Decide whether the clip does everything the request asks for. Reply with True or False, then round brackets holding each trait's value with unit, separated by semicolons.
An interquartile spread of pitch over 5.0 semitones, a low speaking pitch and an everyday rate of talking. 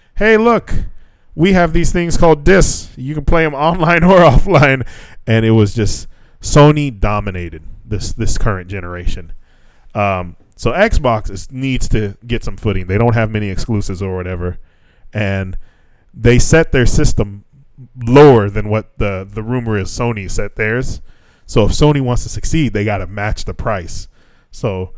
True (5.4 semitones; 110 Hz; 165 wpm)